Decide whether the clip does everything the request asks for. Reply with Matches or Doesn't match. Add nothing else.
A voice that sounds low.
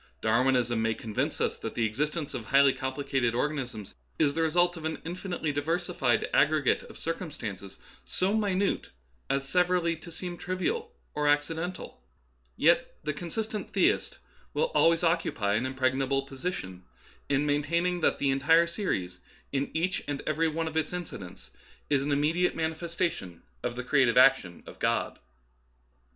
Doesn't match